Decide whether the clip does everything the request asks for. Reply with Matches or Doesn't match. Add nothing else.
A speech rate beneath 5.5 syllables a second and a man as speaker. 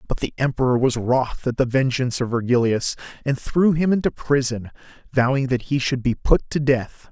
Matches